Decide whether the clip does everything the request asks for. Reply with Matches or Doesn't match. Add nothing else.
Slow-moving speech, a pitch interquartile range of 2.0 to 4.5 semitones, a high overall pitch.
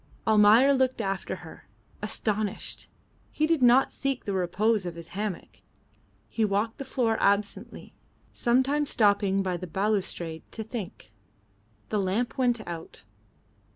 Matches